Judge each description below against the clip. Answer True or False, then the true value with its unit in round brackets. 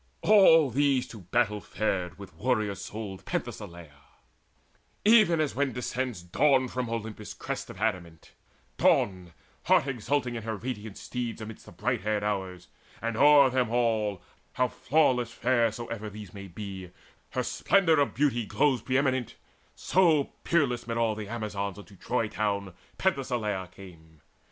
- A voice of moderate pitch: False (115 Hz)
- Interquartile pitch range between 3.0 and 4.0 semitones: False (4.4 semitones)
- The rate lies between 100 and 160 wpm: True (145 wpm)